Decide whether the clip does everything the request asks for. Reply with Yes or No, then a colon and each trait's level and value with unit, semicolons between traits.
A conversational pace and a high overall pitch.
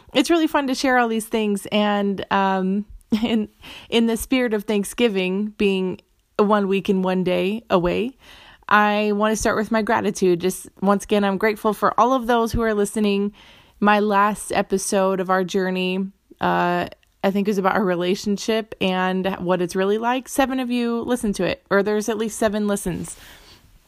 Yes: average, 180 wpm; high, 205 Hz